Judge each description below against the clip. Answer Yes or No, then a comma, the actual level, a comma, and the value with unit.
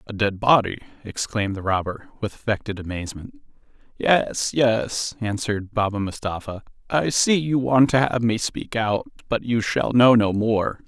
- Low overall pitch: Yes, low, 110 Hz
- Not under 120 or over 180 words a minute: Yes, average, 160 wpm